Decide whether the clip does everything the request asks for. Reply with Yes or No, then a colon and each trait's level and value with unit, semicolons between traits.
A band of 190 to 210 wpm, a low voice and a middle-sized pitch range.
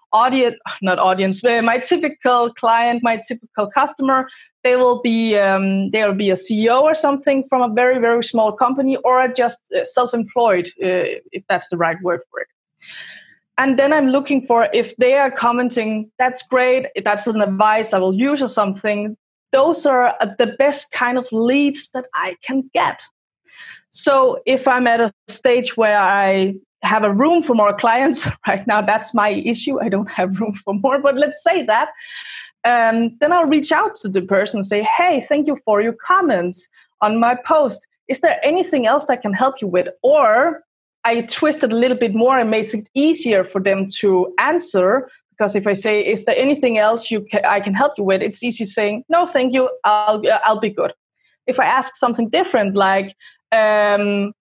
No: average, 195 wpm; high, 235 Hz; average, 4.2 semitones